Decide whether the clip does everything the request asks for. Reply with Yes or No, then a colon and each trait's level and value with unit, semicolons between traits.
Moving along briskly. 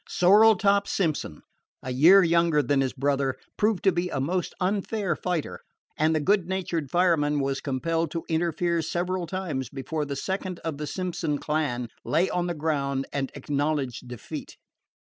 No: average, 160 wpm